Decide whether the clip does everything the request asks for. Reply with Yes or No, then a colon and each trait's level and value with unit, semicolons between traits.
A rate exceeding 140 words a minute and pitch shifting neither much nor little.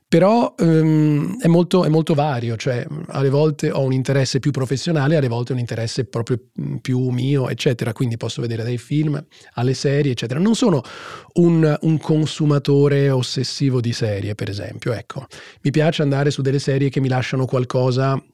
Yes: fast, 170 wpm; average, 3.3 semitones